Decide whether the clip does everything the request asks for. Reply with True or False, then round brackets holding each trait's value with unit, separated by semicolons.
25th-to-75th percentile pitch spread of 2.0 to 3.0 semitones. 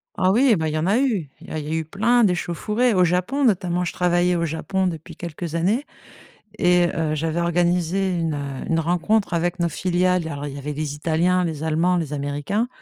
True (2.5 semitones)